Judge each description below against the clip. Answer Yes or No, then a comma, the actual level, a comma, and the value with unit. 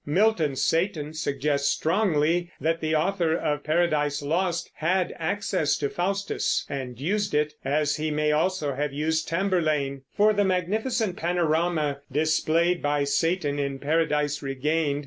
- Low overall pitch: No, medium, 155 Hz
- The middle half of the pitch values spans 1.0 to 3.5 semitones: Yes, average, 3.1 semitones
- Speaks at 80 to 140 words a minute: Yes, slow, 135 wpm